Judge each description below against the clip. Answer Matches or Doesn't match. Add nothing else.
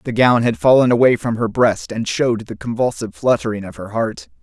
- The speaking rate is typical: Doesn't match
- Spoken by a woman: Doesn't match